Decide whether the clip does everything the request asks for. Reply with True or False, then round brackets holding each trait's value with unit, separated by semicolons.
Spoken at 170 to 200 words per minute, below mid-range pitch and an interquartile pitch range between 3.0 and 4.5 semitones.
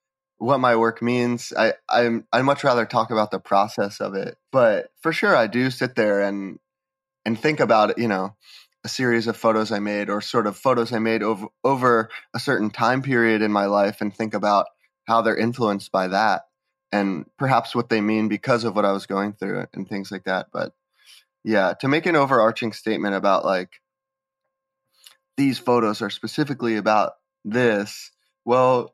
True (185 wpm; 115 Hz; 3.5 semitones)